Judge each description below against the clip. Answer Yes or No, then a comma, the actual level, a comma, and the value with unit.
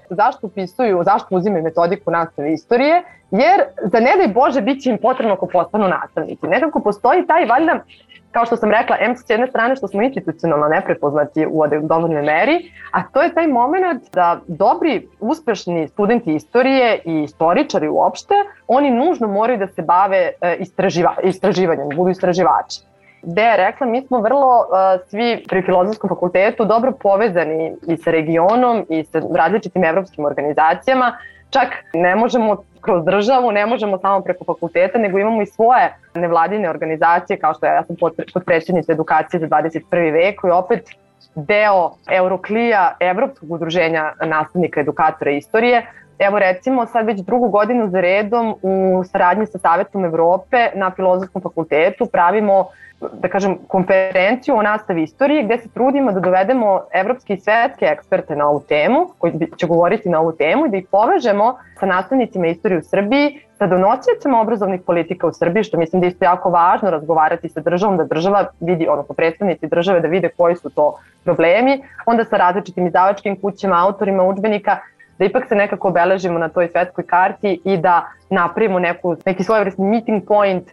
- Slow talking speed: No, average, 165 wpm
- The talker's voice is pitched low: No, high, 190 Hz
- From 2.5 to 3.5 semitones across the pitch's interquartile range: No, average, 4.8 semitones